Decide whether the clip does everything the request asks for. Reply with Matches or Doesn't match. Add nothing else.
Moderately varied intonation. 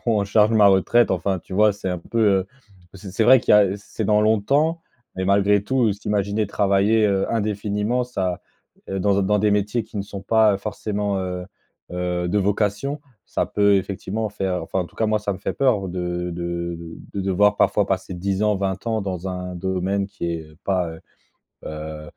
Doesn't match